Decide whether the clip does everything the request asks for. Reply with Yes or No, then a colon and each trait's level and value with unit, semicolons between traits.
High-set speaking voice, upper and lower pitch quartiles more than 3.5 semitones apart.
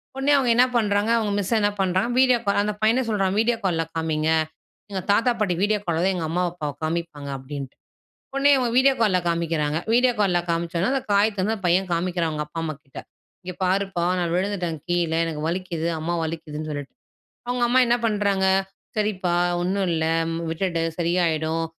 No: medium, 180 Hz; average, 4.1 semitones